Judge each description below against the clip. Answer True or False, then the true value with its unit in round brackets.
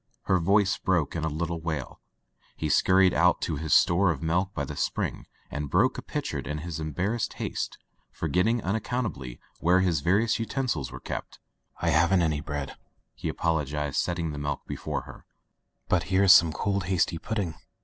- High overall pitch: False (85 Hz)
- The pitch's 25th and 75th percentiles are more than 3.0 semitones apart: True (3.5 semitones)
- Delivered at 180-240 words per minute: True (185 wpm)